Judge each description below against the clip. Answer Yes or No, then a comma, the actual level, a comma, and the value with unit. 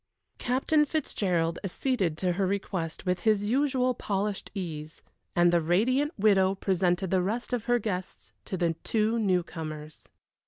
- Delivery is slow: No, average, 150 wpm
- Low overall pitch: No, high, 195 Hz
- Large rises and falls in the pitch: No, average, 4.7 semitones